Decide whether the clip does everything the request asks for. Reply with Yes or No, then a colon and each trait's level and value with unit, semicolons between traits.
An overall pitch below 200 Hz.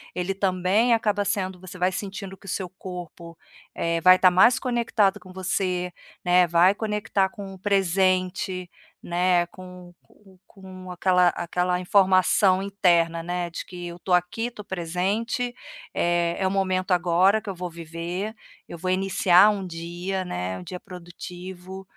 Yes: medium, 185 Hz